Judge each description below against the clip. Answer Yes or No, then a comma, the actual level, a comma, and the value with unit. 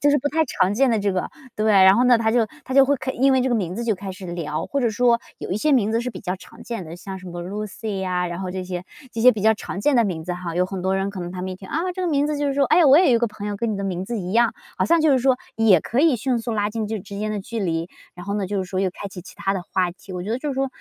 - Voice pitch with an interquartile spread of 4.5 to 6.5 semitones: Yes, average, 4.8 semitones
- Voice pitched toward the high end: Yes, high, 210 Hz